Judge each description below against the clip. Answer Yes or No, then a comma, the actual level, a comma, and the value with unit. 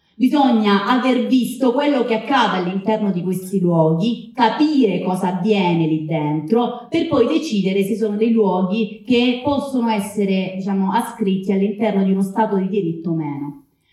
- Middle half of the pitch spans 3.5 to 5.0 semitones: Yes, average, 4.2 semitones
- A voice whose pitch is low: No, high, 210 Hz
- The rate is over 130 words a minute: Yes, average, 150 wpm